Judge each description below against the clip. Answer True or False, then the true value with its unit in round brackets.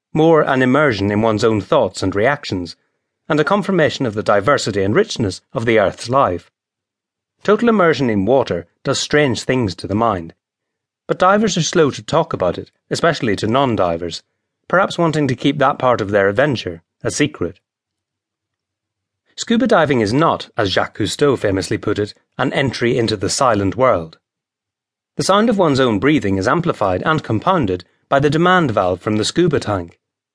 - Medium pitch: False (125 Hz)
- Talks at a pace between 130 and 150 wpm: False (170 wpm)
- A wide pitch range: True (7.0 semitones)